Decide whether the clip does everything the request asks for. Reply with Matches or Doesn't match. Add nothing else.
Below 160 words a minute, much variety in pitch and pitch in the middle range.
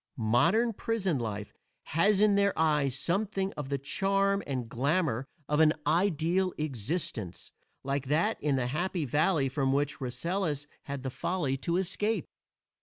Matches